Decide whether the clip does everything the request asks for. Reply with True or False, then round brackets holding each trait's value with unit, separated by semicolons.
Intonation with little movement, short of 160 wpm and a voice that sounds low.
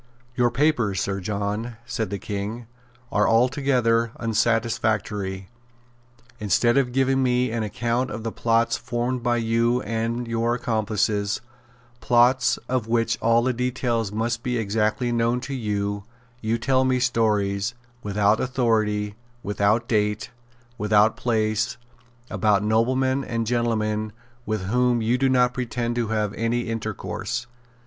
True (2.3 semitones; 135 wpm; 115 Hz)